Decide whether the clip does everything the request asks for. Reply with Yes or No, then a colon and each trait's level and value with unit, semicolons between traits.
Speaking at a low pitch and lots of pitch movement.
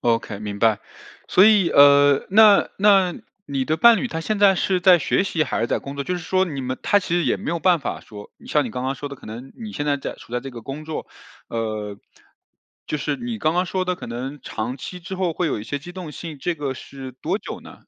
No: medium, 150 Hz; wide, 5.9 semitones